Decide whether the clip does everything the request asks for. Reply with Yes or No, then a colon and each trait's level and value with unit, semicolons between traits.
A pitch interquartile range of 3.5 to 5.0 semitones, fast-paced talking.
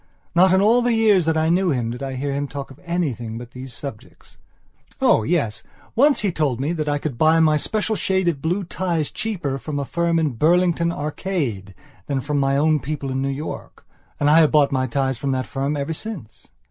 Yes: average, 4.2 semitones; fast, 220 wpm